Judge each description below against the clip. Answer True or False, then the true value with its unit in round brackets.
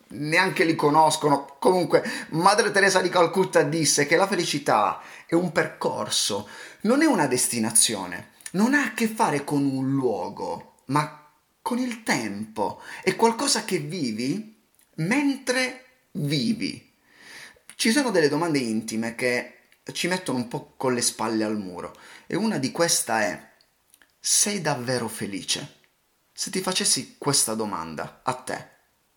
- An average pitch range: False (8.6 semitones)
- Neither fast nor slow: True (140 wpm)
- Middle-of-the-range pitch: True (165 Hz)